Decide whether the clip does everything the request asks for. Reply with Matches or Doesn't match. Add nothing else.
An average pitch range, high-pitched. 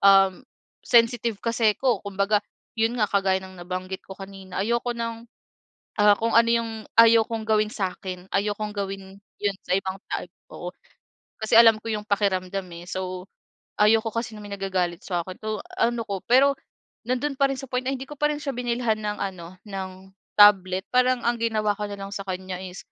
Matches